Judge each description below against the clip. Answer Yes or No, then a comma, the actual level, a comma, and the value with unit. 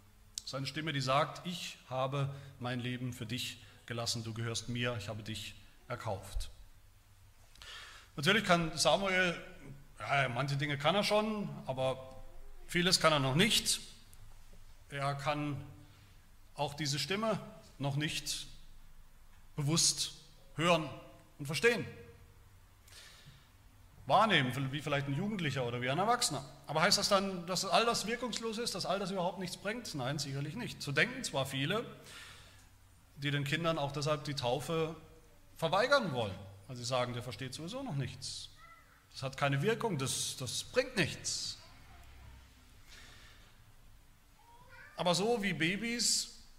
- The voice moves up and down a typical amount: No, wide, 6.5 semitones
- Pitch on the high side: No, medium, 140 Hz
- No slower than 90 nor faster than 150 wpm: Yes, average, 135 wpm